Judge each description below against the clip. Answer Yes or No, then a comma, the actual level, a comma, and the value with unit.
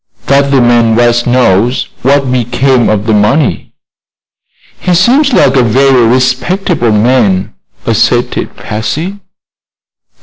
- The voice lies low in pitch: Yes, low, 125 Hz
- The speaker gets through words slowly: Yes, slow, 110 wpm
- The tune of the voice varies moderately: Yes, average, 3.2 semitones